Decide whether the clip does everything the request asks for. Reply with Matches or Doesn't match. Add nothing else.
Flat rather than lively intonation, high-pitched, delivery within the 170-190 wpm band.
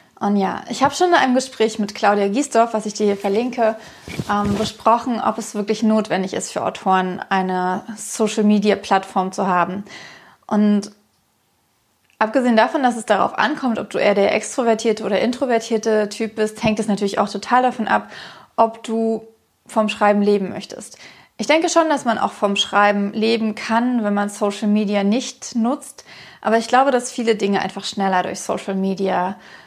Matches